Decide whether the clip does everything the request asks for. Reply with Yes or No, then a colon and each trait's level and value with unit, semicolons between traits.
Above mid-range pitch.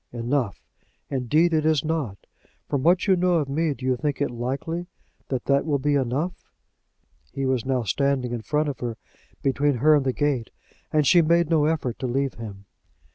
No: medium, 140 Hz